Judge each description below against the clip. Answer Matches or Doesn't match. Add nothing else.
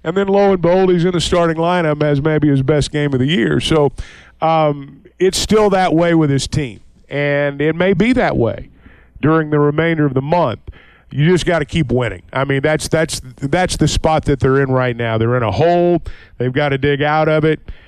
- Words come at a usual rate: Doesn't match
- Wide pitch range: Doesn't match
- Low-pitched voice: Doesn't match